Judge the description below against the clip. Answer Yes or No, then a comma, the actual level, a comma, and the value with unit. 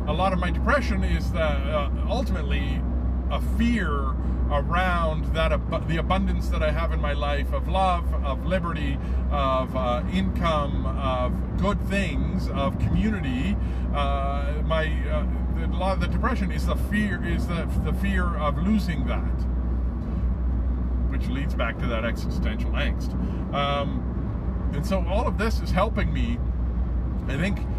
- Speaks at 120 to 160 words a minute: Yes, average, 155 wpm